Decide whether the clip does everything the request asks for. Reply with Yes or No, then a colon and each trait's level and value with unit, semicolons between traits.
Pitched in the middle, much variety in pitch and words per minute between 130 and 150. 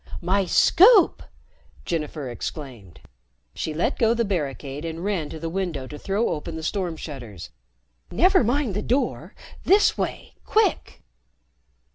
Yes: medium, 170 Hz; wide, 6.9 semitones; slow, 135 wpm